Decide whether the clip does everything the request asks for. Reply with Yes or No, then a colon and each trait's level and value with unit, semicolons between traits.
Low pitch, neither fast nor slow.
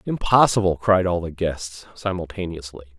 No: very low, 90 Hz; slow, 120 wpm